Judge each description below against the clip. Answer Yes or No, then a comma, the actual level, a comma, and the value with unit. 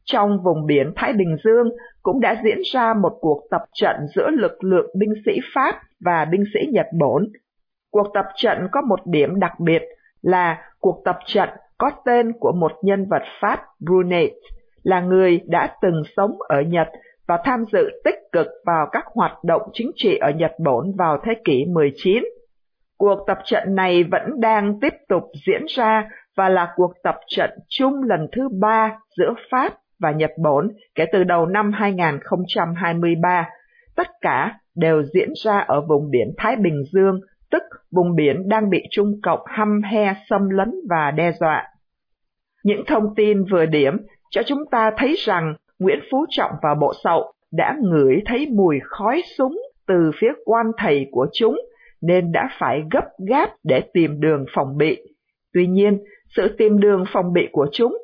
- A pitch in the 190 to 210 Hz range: Yes, high, 200 Hz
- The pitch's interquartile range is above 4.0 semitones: Yes, average, 5.0 semitones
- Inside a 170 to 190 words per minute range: Yes, average, 175 wpm